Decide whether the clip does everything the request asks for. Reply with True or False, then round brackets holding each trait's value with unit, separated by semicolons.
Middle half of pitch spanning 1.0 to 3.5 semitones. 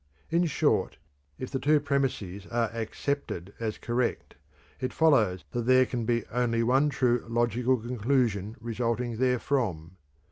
True (2.6 semitones)